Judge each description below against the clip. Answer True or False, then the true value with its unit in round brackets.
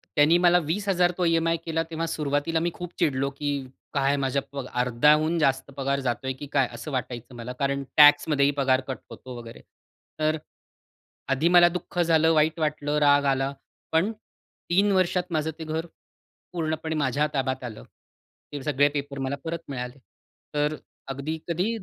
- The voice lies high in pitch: False (150 Hz)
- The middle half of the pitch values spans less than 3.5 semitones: True (3.1 semitones)